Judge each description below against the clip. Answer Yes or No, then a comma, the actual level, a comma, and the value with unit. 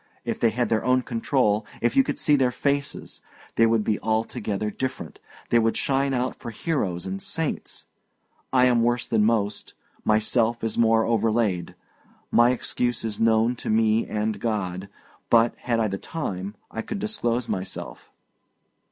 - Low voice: Yes, low, 115 Hz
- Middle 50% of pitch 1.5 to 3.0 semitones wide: Yes, narrow, 2.6 semitones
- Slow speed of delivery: No, average, 160 wpm